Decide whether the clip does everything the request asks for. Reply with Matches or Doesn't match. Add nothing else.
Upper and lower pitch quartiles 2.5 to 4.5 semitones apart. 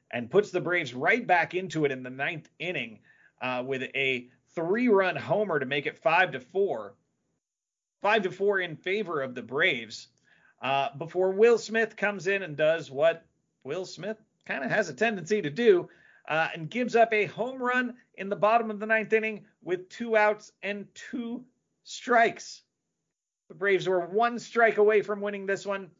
Doesn't match